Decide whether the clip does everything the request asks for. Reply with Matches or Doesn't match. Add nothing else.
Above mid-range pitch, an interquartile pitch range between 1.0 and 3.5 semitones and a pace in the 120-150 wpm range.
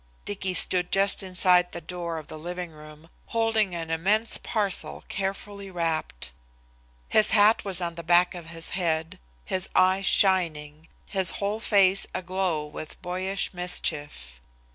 Doesn't match